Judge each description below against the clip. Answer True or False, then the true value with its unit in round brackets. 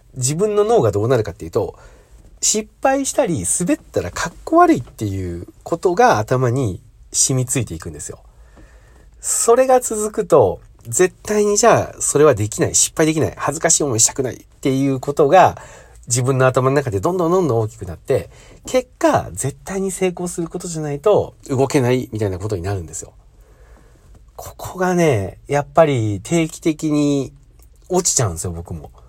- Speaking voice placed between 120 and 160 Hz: True (135 Hz)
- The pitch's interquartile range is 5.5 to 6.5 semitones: False (8.8 semitones)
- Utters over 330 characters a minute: True (350 characters per minute)